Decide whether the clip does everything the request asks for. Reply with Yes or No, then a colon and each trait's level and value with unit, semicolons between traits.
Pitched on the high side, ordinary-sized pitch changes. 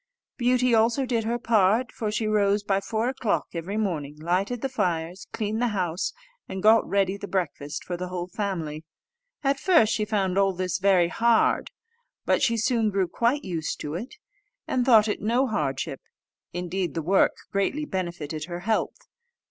Yes: high, 200 Hz; average, 4.4 semitones